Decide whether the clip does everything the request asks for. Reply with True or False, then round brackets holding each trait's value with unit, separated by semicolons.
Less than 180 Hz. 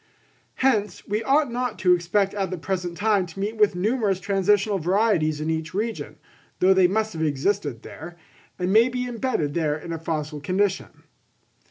False (190 Hz)